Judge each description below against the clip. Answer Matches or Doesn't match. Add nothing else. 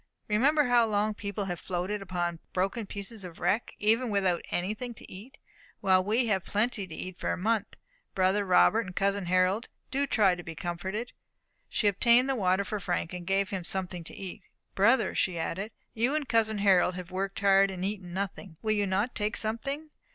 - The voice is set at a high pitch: Matches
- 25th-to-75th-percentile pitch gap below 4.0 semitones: Matches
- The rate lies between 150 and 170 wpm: Doesn't match